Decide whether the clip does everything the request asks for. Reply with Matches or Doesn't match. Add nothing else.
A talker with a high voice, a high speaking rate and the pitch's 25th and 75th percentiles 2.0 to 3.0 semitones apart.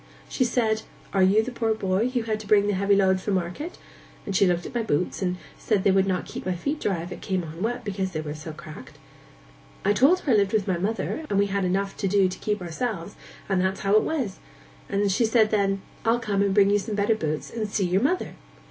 Matches